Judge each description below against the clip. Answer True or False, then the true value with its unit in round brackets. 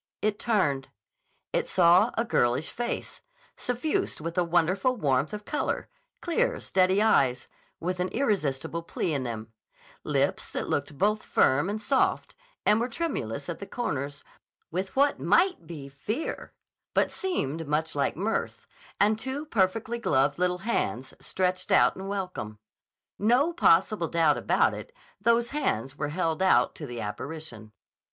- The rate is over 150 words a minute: False (145 wpm)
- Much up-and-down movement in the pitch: True (7.7 semitones)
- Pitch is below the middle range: False (185 Hz)